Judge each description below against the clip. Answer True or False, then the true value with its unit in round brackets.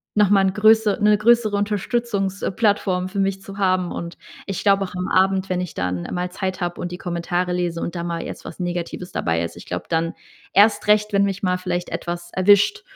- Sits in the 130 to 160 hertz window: False (185 Hz)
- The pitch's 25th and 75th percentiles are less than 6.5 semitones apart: True (2.5 semitones)